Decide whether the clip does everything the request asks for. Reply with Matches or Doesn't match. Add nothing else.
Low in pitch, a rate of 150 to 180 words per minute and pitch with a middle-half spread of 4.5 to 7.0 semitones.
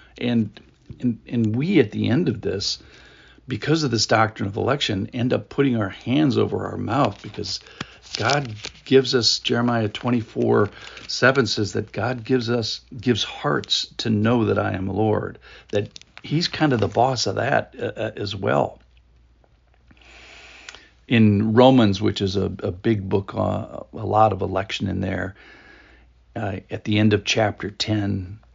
Doesn't match